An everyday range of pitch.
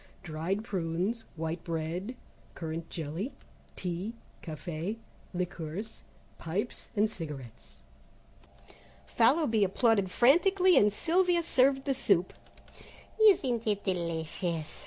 No: wide, 6.3 semitones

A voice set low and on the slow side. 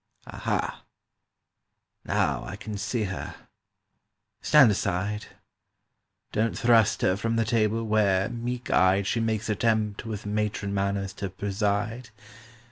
Yes: low, 105 Hz; slow, 115 wpm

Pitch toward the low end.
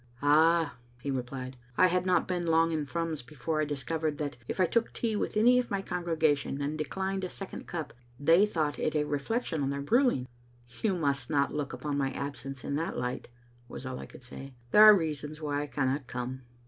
No: medium, 150 Hz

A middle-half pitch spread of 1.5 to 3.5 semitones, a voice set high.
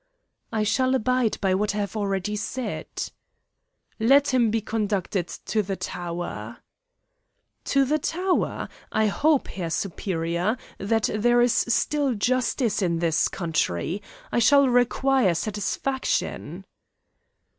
No: average, 5.2 semitones; high, 215 Hz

